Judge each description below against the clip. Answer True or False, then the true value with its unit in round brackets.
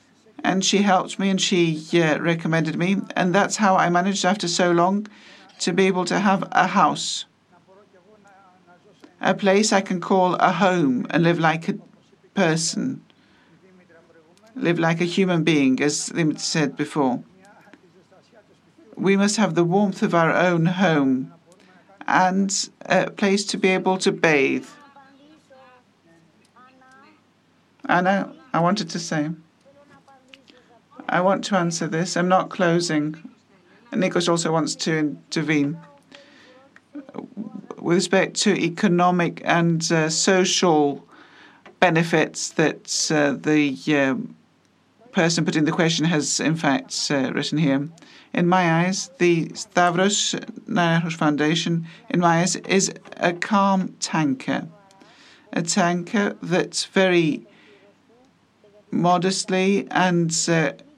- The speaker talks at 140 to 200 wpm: False (120 wpm)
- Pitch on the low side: False (185 Hz)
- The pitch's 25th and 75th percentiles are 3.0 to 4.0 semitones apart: True (3.5 semitones)